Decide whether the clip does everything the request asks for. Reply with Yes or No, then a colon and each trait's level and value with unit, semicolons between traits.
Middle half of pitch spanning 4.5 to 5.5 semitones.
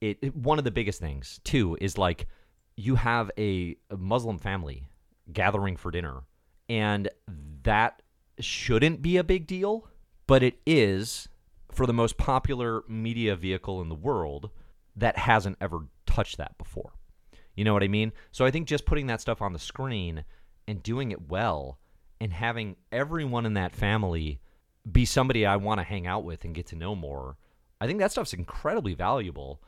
Yes: average, 5.2 semitones